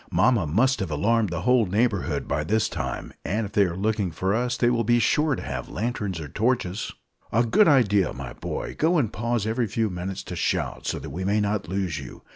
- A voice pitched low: Yes, low, 105 Hz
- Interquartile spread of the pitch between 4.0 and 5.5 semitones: Yes, average, 4.6 semitones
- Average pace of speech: No, fast, 225 wpm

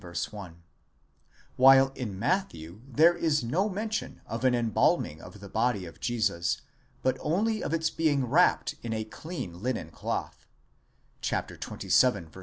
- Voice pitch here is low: Yes, low, 125 Hz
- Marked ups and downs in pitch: Yes, wide, 8.1 semitones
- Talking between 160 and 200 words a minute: No, average, 140 wpm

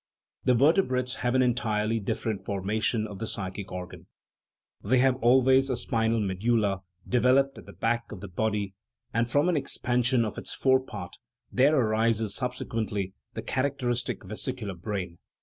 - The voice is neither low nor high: No, low, 115 Hz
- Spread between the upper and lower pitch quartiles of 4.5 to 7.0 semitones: No, average, 3.7 semitones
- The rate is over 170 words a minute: No, average, 160 wpm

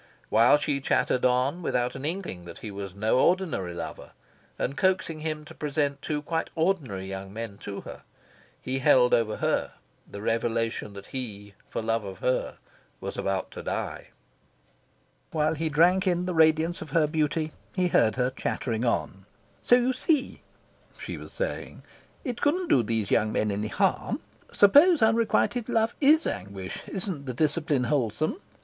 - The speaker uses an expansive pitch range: Yes, wide, 8.0 semitones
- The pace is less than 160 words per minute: No, average, 165 wpm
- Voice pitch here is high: No, medium, 140 Hz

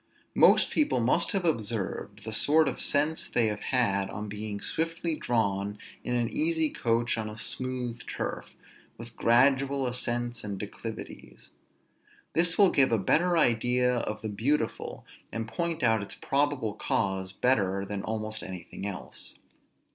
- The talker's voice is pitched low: Yes, low, 115 Hz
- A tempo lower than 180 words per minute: Yes, average, 145 wpm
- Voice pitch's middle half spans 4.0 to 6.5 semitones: Yes, average, 4.7 semitones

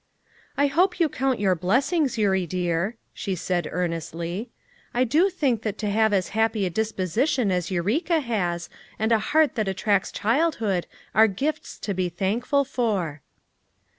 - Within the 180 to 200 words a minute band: No, average, 155 wpm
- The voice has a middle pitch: No, high, 215 Hz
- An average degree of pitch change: No, wide, 6.0 semitones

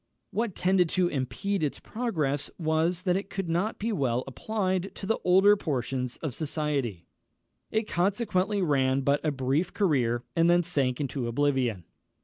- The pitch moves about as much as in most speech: No, wide, 6.2 semitones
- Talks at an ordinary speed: Yes, average, 155 wpm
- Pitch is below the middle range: No, medium, 160 Hz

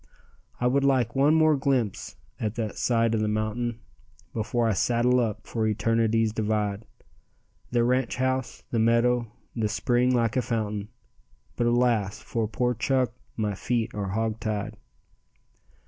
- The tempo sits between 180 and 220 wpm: No, average, 145 wpm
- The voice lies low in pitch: Yes, low, 115 Hz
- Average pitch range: No, narrow, 2.3 semitones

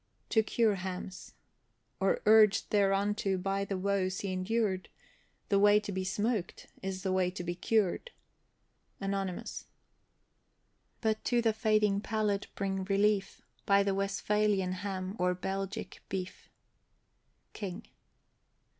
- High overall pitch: Yes, high, 195 Hz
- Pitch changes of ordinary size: No, narrow, 1.8 semitones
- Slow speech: Yes, slow, 120 wpm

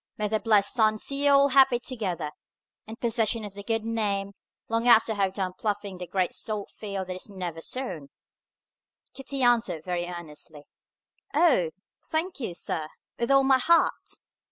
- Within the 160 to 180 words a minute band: Yes, average, 170 wpm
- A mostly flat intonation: No, average, 4.8 semitones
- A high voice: Yes, high, 215 Hz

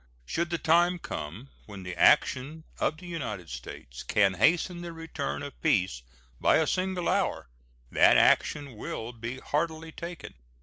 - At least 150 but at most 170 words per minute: Yes, average, 155 wpm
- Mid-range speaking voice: Yes, medium, 145 Hz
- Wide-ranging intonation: Yes, wide, 8.2 semitones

